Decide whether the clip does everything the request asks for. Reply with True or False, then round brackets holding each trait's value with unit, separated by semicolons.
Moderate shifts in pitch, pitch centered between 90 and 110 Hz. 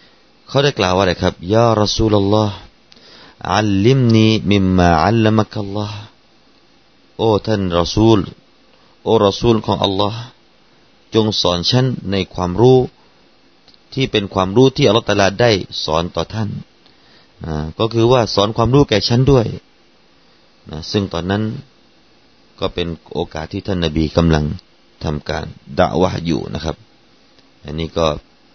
True (4.3 semitones; 100 Hz)